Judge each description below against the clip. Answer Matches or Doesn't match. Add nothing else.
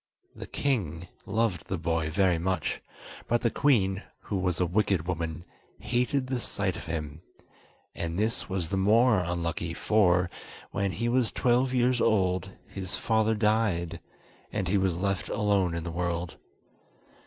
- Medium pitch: Doesn't match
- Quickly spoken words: Doesn't match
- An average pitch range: Matches